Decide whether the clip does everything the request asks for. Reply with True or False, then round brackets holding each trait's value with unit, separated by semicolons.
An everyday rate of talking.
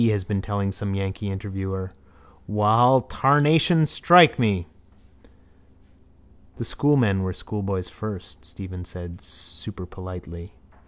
False (100 wpm)